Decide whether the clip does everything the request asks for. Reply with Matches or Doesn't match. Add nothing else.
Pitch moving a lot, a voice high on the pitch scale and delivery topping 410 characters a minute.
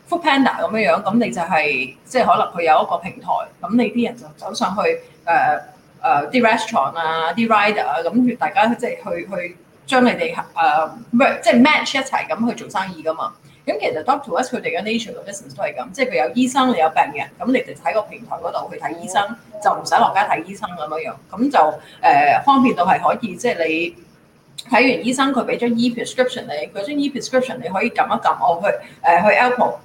Doesn't match